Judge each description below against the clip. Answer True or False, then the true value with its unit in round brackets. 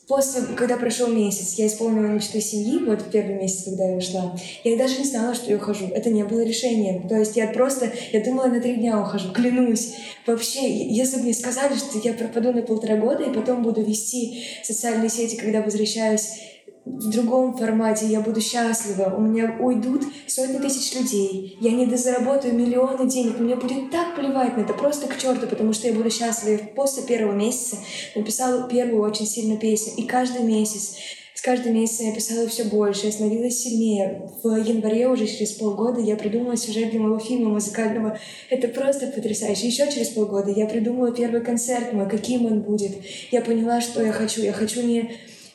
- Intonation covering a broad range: False (2.4 semitones)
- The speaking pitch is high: True (230 Hz)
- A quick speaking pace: True (190 wpm)